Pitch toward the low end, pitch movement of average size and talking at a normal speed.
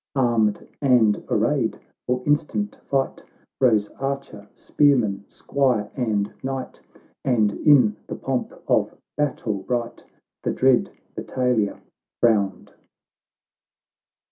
No: low, 125 Hz; average, 4.2 semitones; slow, 95 wpm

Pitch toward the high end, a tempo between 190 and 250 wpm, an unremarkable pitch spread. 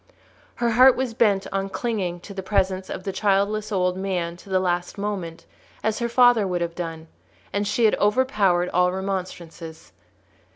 No: high, 195 Hz; average, 170 wpm; average, 3.0 semitones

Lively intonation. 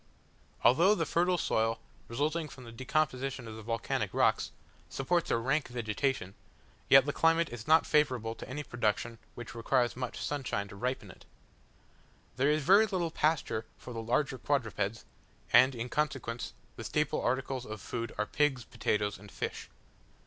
No: average, 4.5 semitones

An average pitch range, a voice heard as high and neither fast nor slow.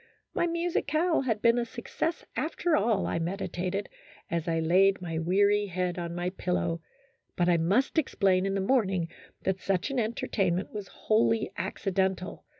Yes: average, 4.4 semitones; high, 195 Hz; average, 155 wpm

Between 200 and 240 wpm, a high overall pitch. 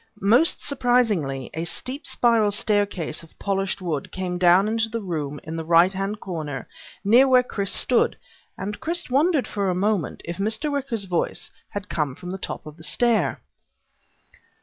No: average, 170 wpm; high, 200 Hz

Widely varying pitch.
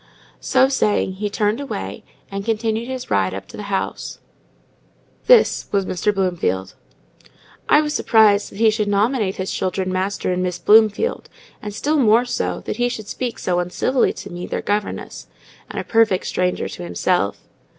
No: average, 3.6 semitones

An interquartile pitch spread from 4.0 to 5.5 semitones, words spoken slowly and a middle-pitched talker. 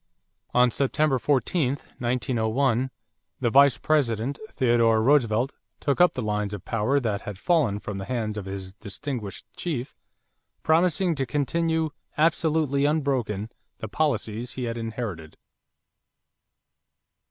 No: average, 4.9 semitones; slow, 120 wpm; low, 125 Hz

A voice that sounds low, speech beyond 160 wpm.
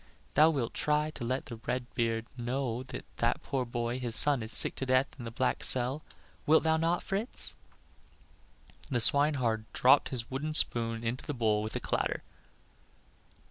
Yes: low, 125 Hz; average, 175 wpm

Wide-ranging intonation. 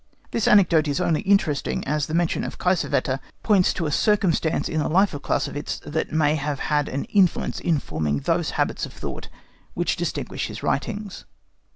No: average, 4.3 semitones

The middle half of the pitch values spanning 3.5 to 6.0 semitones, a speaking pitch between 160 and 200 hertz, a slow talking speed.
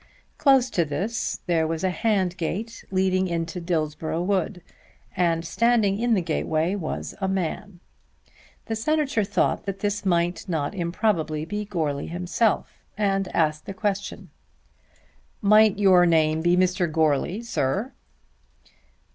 Yes: average, 3.8 semitones; medium, 185 Hz; slow, 130 wpm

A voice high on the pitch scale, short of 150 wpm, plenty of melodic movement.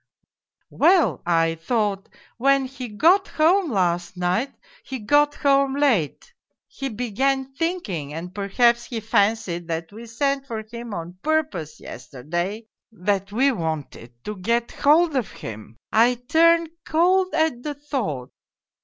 Yes: high, 235 Hz; slow, 135 wpm; wide, 7.6 semitones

